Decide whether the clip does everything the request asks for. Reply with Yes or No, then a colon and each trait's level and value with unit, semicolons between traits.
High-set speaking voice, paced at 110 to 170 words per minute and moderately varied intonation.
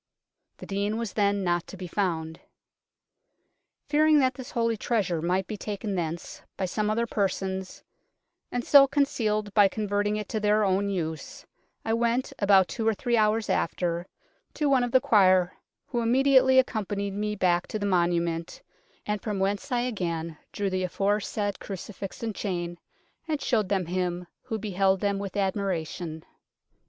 Yes: high, 200 Hz; average, 165 wpm; average, 3.3 semitones